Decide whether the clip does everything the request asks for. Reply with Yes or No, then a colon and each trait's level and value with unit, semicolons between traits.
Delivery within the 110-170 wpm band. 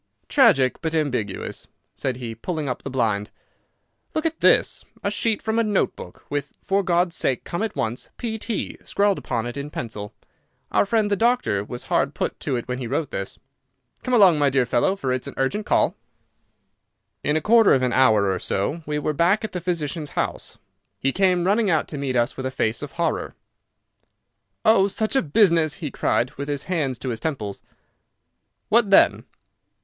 No: average, 185 wpm